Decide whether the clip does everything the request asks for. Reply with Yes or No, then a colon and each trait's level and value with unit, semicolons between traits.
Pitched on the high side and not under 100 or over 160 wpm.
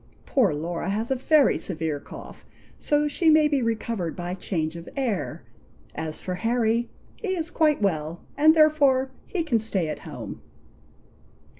Yes: high, 230 Hz; average, 155 wpm